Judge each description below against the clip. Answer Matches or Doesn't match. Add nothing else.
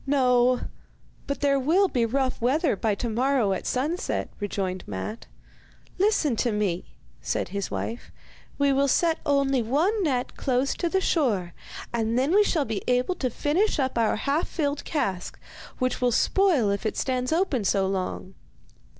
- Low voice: Doesn't match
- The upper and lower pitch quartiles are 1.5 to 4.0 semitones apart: Doesn't match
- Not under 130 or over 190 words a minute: Matches